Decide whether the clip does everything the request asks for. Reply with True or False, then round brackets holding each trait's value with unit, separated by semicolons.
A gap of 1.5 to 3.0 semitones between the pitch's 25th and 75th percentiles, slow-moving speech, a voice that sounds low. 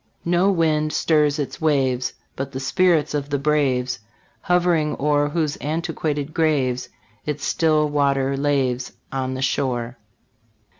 False (2.6 semitones; 130 wpm; 145 Hz)